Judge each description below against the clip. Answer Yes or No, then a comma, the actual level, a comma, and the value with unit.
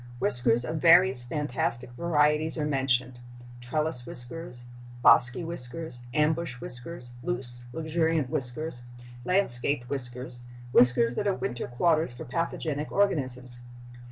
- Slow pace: Yes, slow, 105 wpm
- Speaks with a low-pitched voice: Yes, low, 130 Hz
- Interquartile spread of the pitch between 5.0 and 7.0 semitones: No, average, 4.6 semitones